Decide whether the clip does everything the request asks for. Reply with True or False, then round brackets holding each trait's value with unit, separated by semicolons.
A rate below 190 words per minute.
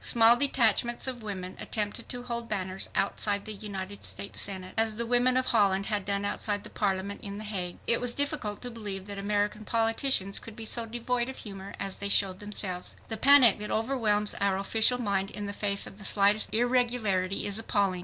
False (200 wpm)